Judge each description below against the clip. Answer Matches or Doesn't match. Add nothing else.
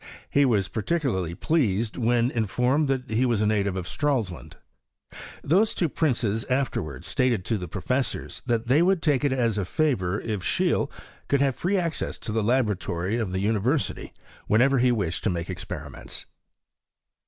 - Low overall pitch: Matches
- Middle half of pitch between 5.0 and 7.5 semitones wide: Matches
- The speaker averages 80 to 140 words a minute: Doesn't match